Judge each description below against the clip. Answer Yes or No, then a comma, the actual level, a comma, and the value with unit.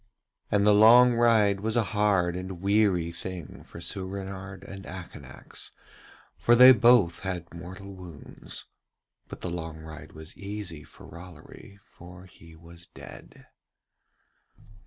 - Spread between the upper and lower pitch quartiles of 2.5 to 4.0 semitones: Yes, average, 3.3 semitones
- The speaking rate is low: Yes, slow, 130 wpm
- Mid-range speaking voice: No, very low, 95 Hz